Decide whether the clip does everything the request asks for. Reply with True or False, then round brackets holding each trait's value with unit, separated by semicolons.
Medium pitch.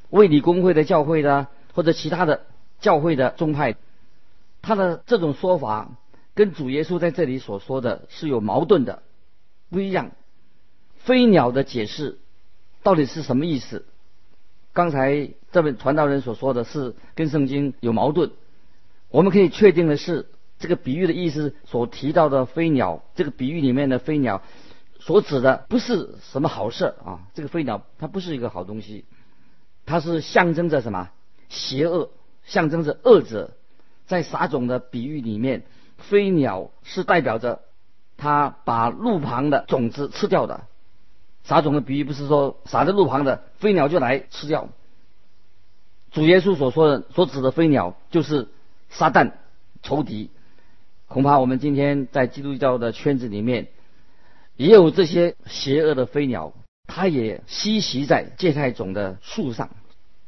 True (145 Hz)